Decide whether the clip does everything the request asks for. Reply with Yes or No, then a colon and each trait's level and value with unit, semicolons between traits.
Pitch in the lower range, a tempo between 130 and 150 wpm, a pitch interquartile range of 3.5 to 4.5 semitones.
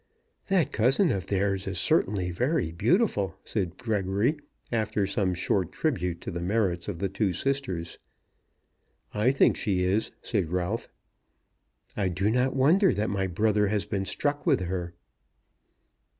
Yes: low, 100 Hz; average, 145 wpm; average, 4.2 semitones